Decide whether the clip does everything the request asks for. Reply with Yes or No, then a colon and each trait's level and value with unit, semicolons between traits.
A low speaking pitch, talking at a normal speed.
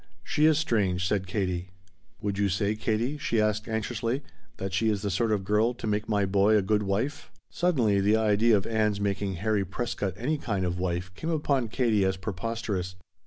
Yes: low, 105 Hz; average, 195 wpm